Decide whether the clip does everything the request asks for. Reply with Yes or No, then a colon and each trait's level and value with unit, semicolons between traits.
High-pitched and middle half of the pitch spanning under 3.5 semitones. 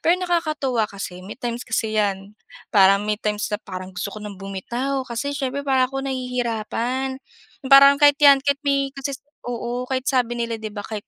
No: high, 245 Hz; average, 4.5 semitones